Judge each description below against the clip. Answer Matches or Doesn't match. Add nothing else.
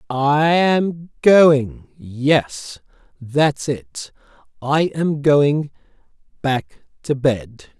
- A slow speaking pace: Matches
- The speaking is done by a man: Matches